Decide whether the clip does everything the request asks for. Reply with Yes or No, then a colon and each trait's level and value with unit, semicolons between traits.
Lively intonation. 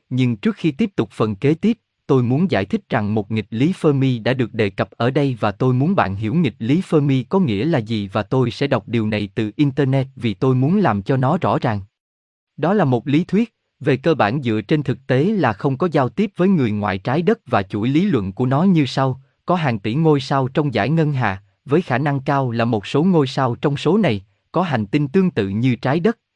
Yes: wide, 5.8 semitones